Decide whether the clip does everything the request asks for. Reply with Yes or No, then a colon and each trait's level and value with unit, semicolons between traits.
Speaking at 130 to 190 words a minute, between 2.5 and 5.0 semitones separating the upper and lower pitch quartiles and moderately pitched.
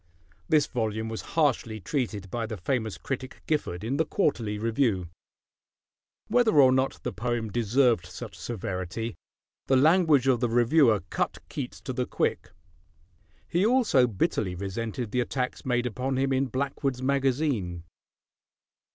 No: average, 140 wpm; average, 3.9 semitones; low, 125 Hz